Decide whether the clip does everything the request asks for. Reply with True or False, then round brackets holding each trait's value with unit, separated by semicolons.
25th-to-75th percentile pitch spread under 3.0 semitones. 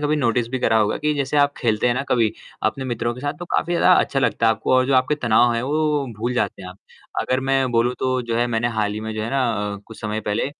False (3.4 semitones)